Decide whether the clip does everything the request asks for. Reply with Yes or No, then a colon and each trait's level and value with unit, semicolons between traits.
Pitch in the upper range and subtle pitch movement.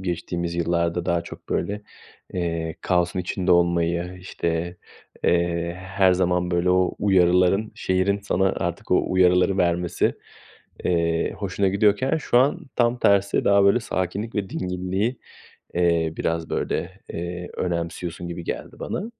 No: very low, 90 Hz; narrow, 2.1 semitones